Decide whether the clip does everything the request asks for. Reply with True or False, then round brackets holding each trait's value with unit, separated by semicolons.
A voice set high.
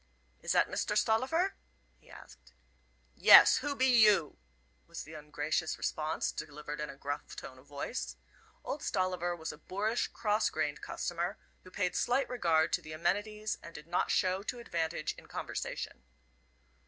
False (175 Hz)